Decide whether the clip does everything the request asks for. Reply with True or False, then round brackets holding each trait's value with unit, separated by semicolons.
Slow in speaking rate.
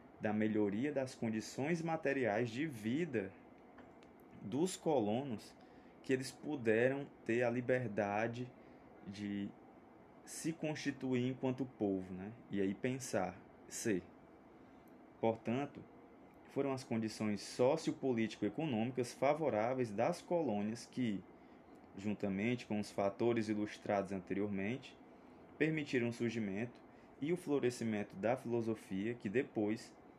True (100 wpm)